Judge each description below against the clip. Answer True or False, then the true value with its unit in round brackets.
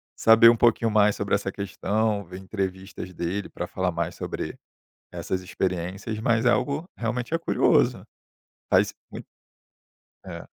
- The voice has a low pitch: True (100 Hz)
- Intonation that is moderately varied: True (3.4 semitones)